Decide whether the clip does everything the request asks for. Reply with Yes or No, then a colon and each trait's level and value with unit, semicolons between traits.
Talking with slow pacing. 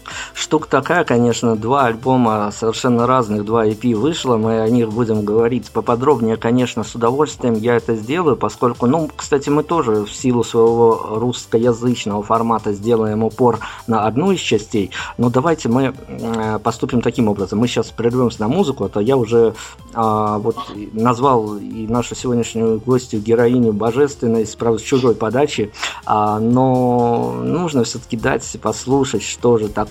No: average, 145 wpm